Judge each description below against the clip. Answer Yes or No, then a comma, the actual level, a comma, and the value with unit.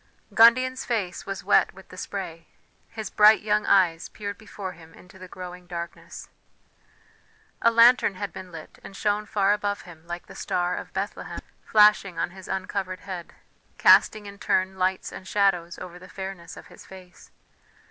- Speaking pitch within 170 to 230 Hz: Yes, high, 190 Hz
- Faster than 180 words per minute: No, average, 170 wpm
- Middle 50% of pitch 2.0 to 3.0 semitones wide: Yes, narrow, 2.5 semitones